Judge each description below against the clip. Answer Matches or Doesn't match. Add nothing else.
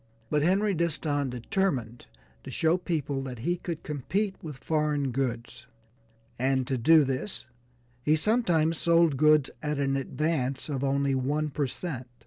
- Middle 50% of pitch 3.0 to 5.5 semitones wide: Matches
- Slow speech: Doesn't match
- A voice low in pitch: Doesn't match